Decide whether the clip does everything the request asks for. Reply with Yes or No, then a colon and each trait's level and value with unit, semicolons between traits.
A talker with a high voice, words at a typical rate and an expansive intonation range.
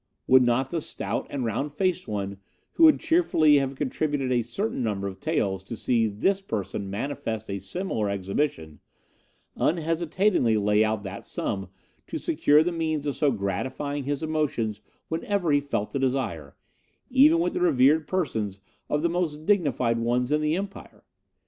No: low, 135 Hz; average, 160 wpm; wide, 6.8 semitones